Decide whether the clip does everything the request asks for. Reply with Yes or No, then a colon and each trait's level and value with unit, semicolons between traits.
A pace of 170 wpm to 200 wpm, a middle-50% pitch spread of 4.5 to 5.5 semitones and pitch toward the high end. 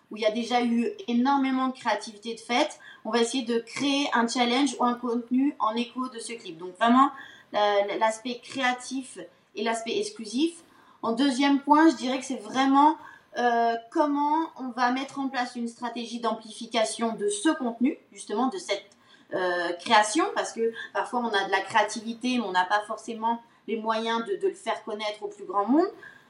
No: average, 185 wpm; average, 3.6 semitones; high, 235 Hz